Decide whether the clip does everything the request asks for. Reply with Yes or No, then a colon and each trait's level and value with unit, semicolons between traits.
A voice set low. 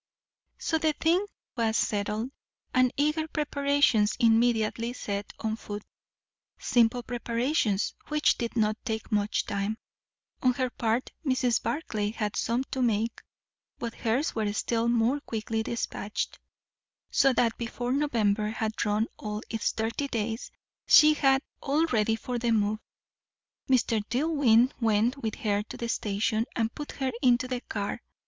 No: high, 230 Hz